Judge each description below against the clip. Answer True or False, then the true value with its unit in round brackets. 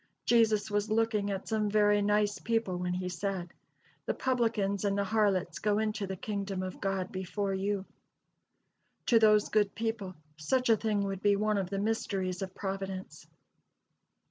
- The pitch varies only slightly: True (1.9 semitones)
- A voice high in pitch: True (205 Hz)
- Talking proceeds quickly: False (165 wpm)